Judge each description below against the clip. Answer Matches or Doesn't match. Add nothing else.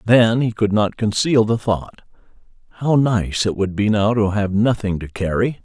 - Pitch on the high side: Doesn't match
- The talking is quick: Doesn't match